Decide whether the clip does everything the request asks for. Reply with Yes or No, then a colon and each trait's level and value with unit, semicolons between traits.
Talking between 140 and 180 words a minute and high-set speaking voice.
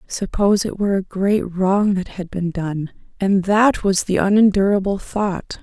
Yes: average, 170 wpm; high, 195 Hz